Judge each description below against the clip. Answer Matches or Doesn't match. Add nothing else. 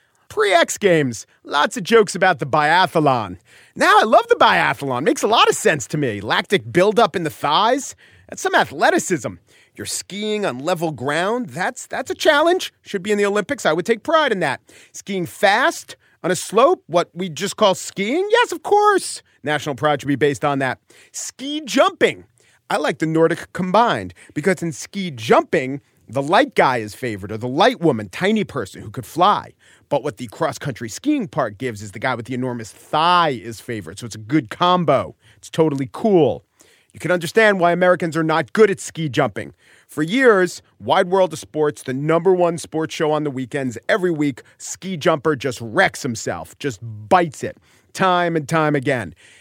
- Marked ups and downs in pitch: Matches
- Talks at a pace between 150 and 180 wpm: Doesn't match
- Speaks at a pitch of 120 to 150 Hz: Doesn't match